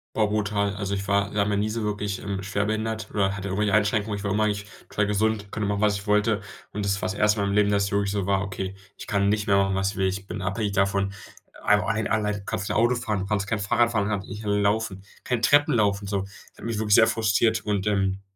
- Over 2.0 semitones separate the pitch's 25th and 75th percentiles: No, narrow, 1.4 semitones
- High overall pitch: No, low, 100 Hz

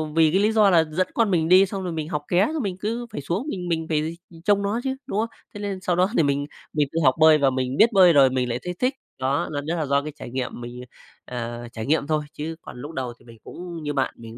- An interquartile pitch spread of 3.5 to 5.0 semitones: No, wide, 5.4 semitones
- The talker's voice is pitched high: No, medium, 160 Hz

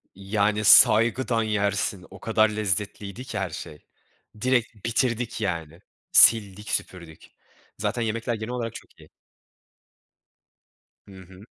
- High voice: No, low, 105 Hz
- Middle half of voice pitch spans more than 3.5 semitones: No, average, 2.9 semitones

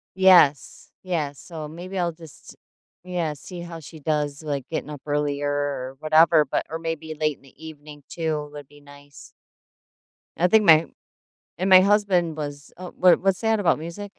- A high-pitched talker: No, medium, 155 Hz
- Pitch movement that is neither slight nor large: Yes, average, 3.2 semitones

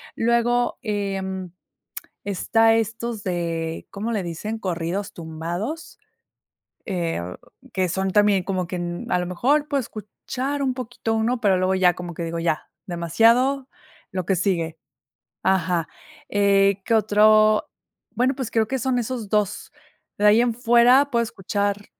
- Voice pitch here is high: Yes, high, 205 Hz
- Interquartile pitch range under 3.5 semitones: No, average, 4.4 semitones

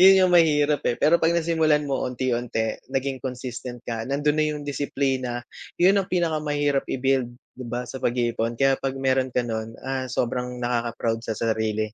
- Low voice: Yes, low, 130 Hz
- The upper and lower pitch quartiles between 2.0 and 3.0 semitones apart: No, average, 3.4 semitones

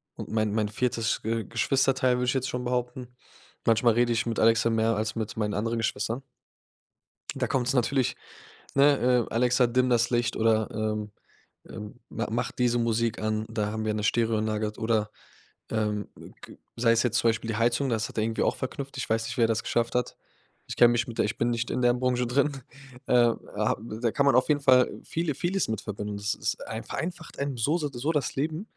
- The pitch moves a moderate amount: No, narrow, 2.3 semitones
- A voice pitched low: Yes, low, 115 Hz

